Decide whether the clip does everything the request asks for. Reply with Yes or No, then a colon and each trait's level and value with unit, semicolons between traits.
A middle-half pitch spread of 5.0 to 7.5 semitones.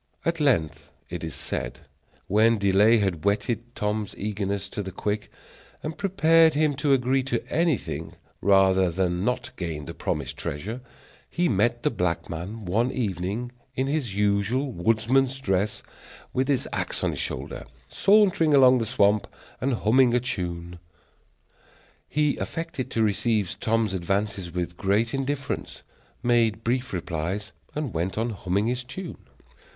Yes: average, 5.3 semitones